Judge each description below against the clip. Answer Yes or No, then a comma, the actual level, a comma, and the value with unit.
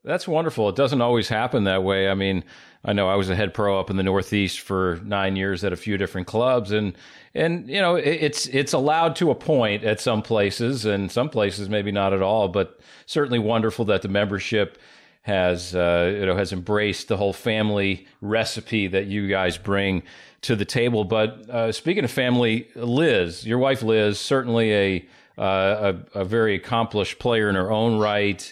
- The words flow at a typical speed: Yes, average, 195 wpm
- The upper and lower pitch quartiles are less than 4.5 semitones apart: Yes, average, 3.2 semitones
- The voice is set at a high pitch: No, low, 105 Hz